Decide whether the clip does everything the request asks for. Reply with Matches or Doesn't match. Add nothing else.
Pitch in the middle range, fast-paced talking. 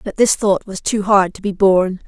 Doesn't match